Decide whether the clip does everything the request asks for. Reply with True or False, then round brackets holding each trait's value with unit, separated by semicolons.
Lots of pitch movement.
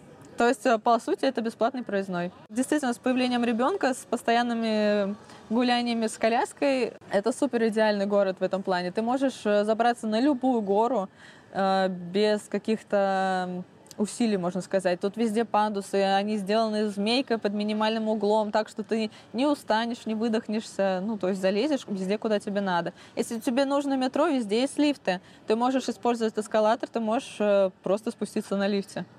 False (3.0 semitones)